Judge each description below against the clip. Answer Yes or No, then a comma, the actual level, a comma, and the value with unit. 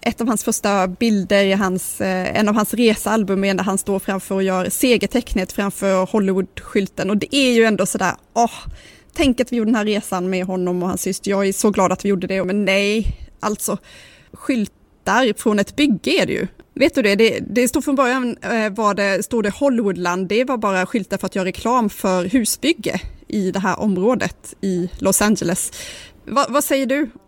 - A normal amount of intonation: Yes, average, 3.6 semitones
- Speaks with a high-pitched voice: Yes, high, 205 Hz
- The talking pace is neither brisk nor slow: No, fast, 200 wpm